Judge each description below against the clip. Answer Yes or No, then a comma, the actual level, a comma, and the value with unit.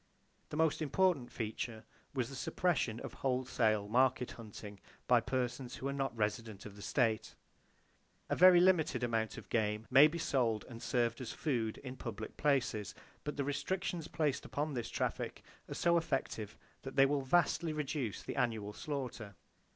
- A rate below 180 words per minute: Yes, average, 165 wpm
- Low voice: Yes, low, 125 Hz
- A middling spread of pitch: Yes, average, 4.7 semitones